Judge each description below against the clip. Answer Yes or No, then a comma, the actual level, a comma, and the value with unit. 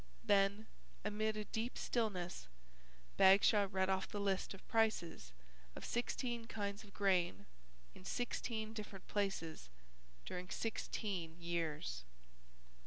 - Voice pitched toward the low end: No, high, 200 Hz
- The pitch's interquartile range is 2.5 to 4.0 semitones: Yes, average, 3.2 semitones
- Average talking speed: No, slow, 110 wpm